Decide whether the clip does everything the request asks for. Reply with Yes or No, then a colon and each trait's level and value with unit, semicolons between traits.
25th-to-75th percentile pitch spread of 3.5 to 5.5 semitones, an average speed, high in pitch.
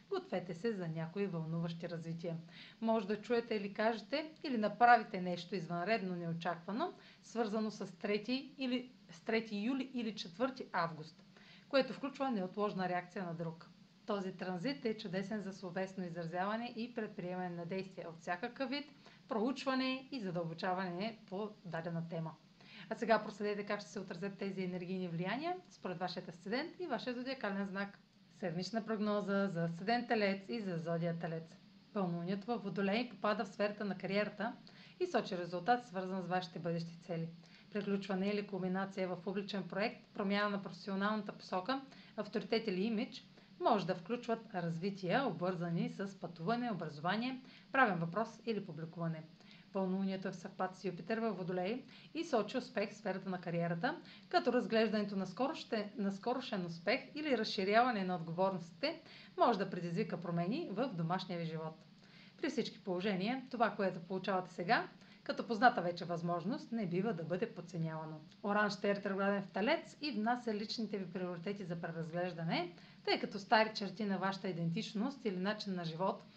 Yes: average, 3.8 semitones; average, 150 wpm; high, 200 Hz